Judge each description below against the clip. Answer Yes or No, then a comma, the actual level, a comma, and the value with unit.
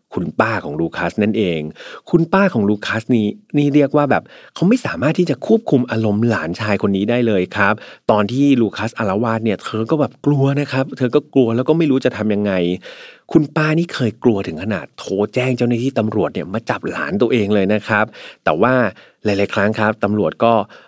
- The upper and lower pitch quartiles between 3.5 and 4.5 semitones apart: No, average, 5.1 semitones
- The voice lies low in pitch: Yes, low, 115 Hz